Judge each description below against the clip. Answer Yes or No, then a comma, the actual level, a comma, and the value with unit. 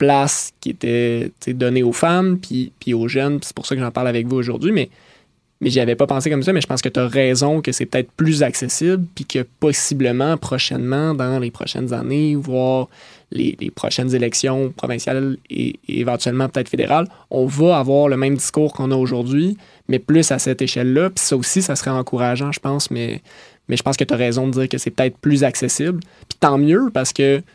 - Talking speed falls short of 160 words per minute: No, fast, 220 wpm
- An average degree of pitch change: No, narrow, 2.3 semitones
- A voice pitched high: No, low, 130 Hz